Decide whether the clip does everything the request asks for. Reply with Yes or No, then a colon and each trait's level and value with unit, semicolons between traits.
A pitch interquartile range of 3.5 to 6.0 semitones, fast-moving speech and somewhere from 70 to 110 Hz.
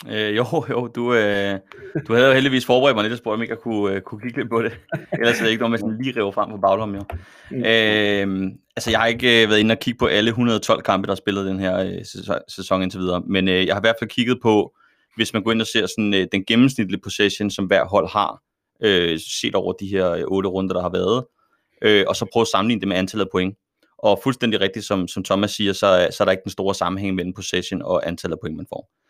No: average, 3.0 semitones; fast, 260 wpm; low, 105 Hz